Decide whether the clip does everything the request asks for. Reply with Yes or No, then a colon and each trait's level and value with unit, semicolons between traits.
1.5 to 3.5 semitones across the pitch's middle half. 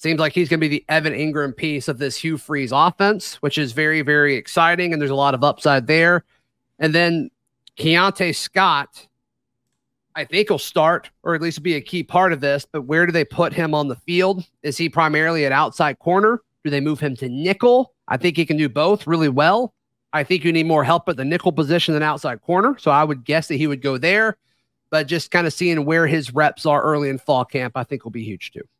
Yes: average, 2.9 semitones